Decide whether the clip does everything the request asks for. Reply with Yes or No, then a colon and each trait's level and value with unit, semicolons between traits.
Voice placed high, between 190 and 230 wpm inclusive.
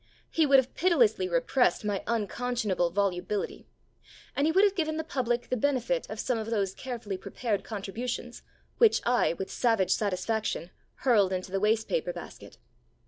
No: high, 235 Hz; average, 160 wpm